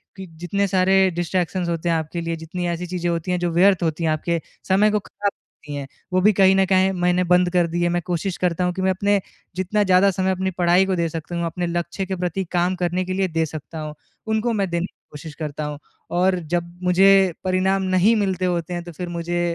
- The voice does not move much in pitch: Yes, narrow, 1.9 semitones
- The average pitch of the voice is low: No, medium, 180 Hz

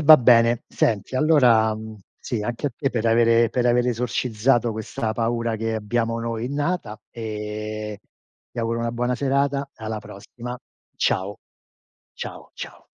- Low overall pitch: Yes, low, 115 Hz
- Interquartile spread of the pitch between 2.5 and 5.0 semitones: No, narrow, 2.0 semitones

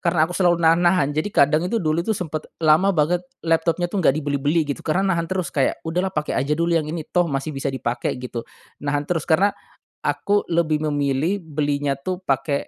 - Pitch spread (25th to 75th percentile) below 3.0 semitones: No, average, 3.3 semitones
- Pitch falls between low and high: Yes, medium, 160 Hz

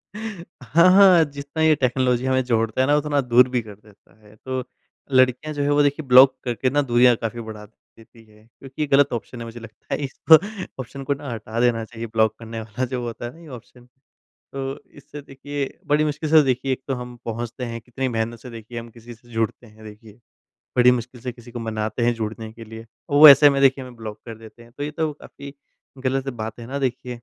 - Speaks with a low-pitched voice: Yes, low, 125 Hz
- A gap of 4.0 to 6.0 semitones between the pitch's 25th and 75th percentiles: No, average, 3.3 semitones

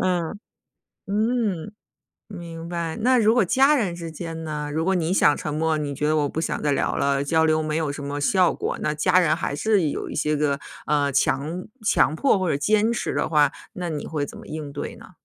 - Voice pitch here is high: No, medium, 160 Hz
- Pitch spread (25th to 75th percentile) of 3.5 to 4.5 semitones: Yes, average, 3.8 semitones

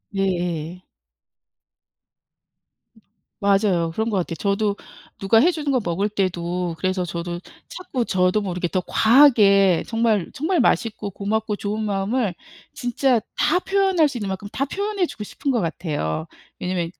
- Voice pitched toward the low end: No, high, 200 Hz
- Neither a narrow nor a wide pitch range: Yes, average, 4.9 semitones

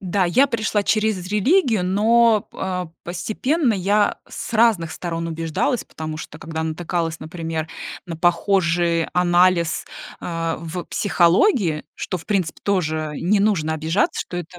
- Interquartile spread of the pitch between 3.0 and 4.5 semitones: Yes, average, 3.9 semitones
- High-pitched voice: No, medium, 180 Hz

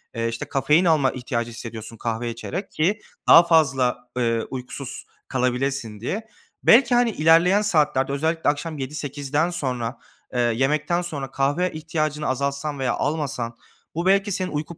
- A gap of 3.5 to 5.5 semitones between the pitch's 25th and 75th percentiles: Yes, average, 4.6 semitones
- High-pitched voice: No, medium, 145 Hz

